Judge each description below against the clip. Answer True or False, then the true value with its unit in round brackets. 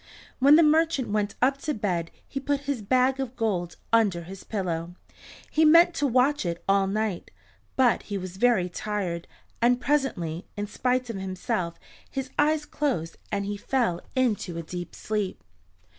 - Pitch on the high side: True (220 Hz)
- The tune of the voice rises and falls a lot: True (6.3 semitones)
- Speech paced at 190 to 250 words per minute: False (160 wpm)